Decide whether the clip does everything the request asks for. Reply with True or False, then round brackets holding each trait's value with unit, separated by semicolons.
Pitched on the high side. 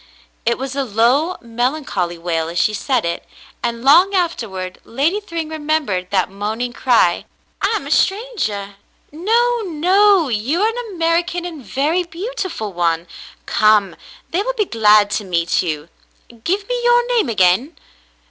True (270 Hz)